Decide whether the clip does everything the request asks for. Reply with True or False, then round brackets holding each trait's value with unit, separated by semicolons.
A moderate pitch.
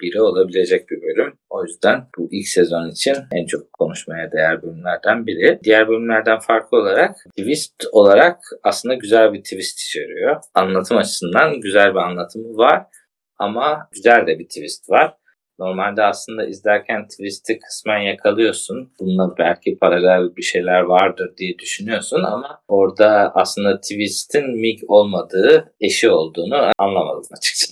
False (110 Hz)